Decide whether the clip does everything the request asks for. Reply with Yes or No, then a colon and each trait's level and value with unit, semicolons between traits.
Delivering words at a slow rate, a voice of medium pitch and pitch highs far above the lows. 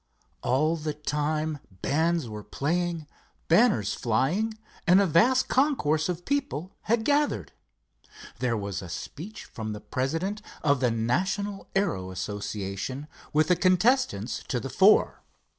Yes: slow, 130 wpm; medium, 155 Hz; wide, 8.2 semitones